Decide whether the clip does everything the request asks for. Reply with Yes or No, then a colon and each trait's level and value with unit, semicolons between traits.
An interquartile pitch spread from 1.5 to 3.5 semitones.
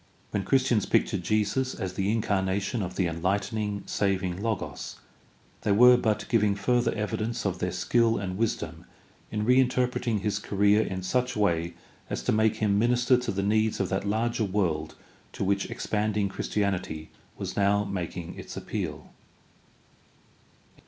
Yes: average, 2.7 semitones